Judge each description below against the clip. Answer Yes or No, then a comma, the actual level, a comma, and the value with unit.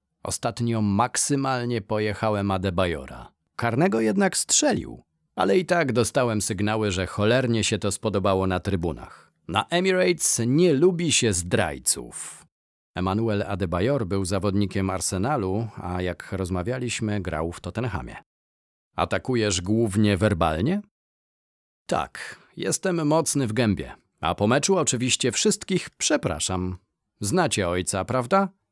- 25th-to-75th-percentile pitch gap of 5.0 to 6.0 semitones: Yes, wide, 5.4 semitones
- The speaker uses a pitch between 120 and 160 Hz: No, low, 110 Hz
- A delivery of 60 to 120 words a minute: Yes, slow, 110 wpm